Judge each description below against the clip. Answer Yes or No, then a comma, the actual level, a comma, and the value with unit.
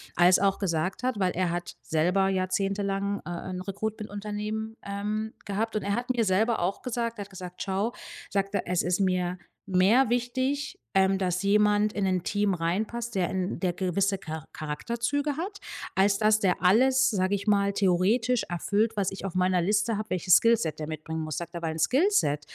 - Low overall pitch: No, high, 200 Hz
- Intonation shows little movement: No, average, 3.1 semitones